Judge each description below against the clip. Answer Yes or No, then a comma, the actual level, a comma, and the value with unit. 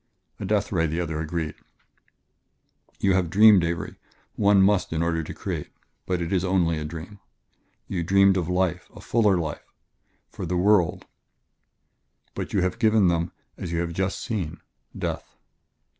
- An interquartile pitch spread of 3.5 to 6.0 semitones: No, average, 2.8 semitones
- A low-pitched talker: Yes, very low, 90 Hz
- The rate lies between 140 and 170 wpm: Yes, average, 165 wpm